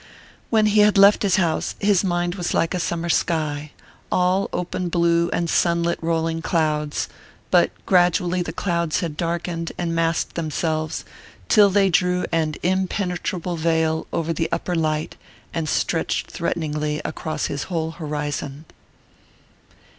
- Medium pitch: Yes, medium, 170 Hz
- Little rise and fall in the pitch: Yes, narrow, 2.1 semitones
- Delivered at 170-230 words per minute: No, average, 140 wpm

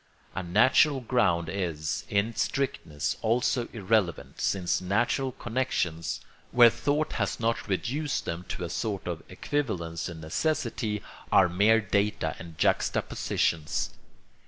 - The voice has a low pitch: Yes, low, 100 Hz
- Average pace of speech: No, slow, 120 wpm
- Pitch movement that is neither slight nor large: No, wide, 5.8 semitones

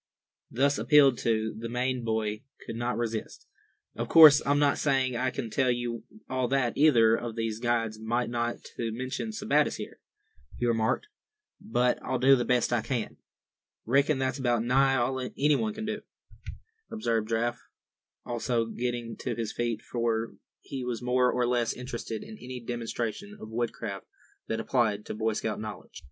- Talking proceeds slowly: No, average, 165 wpm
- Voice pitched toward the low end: Yes, low, 120 Hz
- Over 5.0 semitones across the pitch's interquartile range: No, narrow, 2.4 semitones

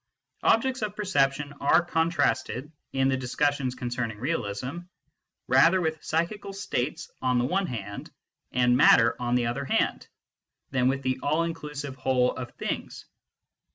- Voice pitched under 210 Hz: Yes, low, 135 Hz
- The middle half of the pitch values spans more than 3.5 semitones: Yes, average, 4.6 semitones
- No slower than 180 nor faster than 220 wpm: No, average, 145 wpm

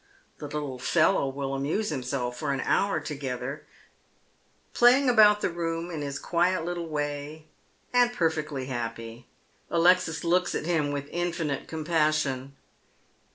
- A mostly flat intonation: No, average, 3.9 semitones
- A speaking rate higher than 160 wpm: No, slow, 135 wpm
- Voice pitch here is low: No, medium, 155 Hz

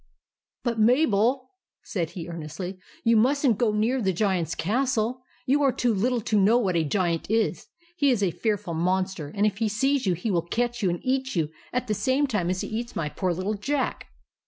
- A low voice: No, high, 215 Hz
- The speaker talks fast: Yes, fast, 210 wpm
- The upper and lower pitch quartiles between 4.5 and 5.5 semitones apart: Yes, average, 5.2 semitones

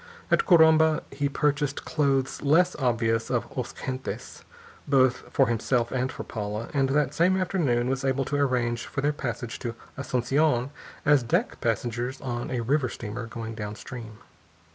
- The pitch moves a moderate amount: Yes, average, 3.3 semitones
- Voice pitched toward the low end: Yes, low, 130 Hz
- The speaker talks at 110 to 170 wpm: Yes, average, 155 wpm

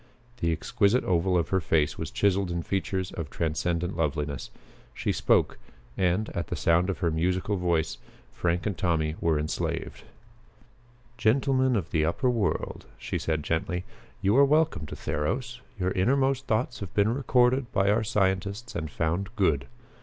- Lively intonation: No, average, 4.9 semitones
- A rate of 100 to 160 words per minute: Yes, average, 155 wpm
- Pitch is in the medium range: No, very low, 95 Hz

